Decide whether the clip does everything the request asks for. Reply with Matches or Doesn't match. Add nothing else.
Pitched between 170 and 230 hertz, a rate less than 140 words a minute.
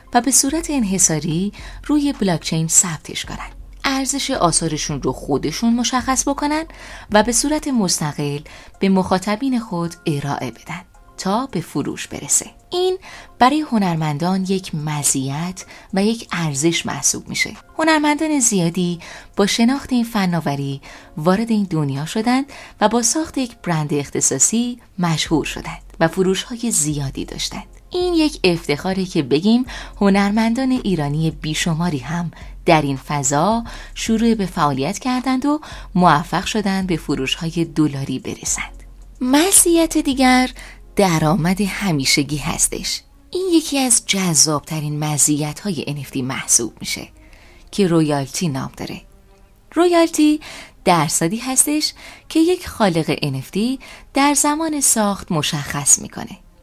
Matches